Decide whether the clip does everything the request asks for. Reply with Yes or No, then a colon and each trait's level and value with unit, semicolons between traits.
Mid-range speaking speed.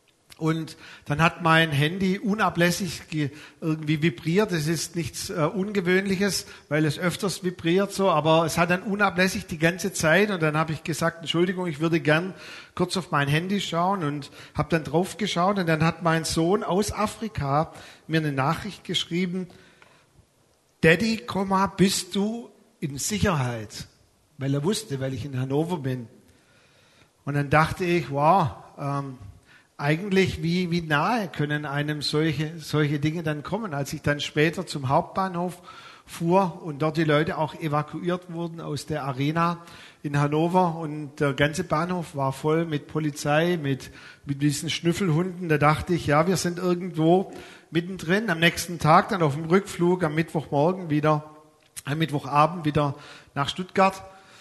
Yes: average, 155 wpm